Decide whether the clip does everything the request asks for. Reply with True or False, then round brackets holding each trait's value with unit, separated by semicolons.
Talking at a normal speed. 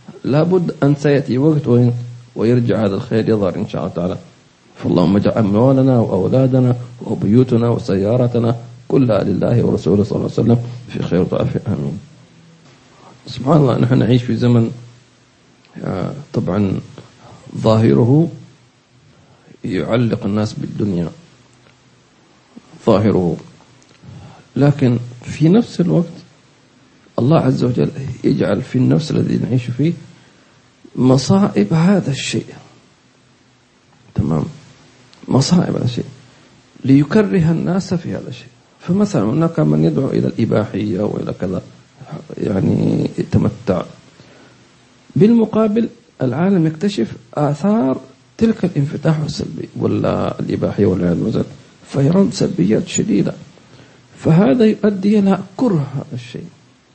False (100 wpm)